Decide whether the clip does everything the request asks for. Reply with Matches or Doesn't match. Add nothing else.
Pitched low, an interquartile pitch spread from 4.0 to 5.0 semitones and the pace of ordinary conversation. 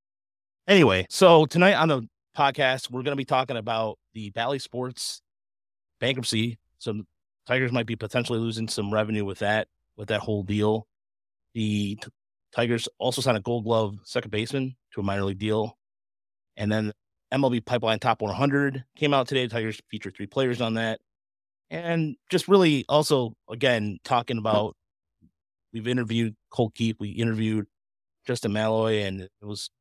Doesn't match